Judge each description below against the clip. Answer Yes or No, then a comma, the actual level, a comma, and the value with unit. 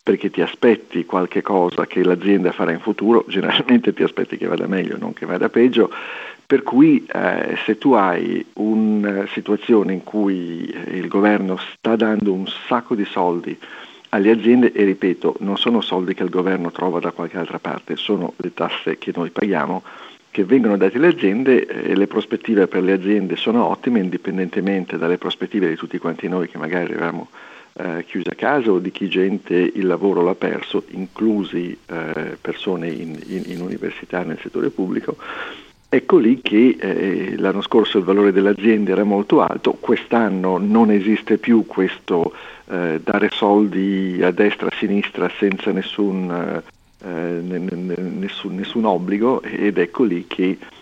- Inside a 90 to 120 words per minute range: No, average, 165 wpm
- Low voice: Yes, very low, 95 Hz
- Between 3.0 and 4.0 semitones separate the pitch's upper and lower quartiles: No, narrow, 2.4 semitones